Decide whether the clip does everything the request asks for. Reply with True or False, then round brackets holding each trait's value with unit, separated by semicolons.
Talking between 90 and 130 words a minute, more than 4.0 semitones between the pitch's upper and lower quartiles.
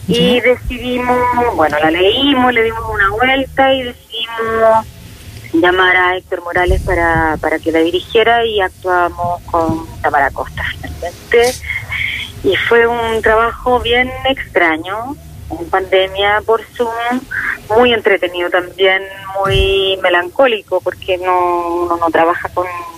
True (125 wpm; 5.1 semitones)